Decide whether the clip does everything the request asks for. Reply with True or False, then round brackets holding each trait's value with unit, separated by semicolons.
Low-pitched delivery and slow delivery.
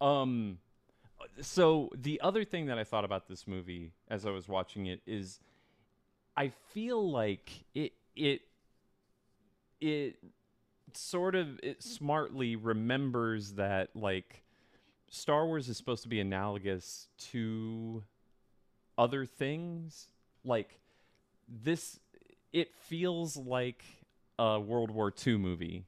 True (120 Hz; 115 wpm)